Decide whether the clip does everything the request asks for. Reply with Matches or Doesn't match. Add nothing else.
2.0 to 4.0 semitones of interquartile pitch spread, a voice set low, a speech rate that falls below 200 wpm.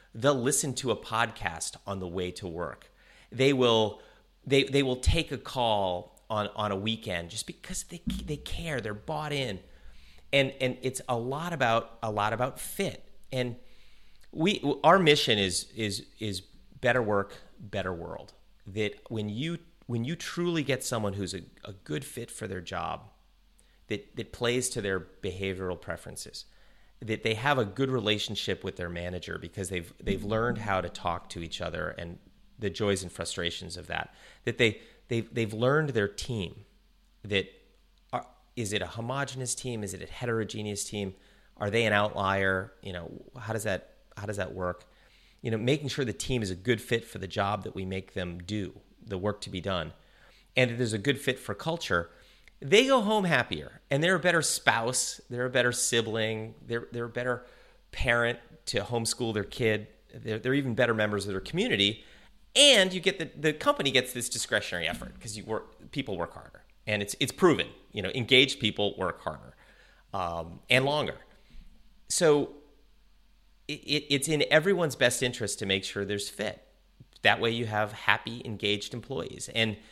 Doesn't match